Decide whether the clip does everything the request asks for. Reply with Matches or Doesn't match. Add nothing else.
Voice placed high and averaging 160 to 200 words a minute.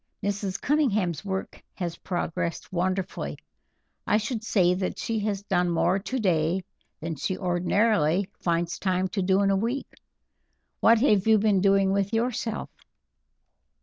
Doesn't match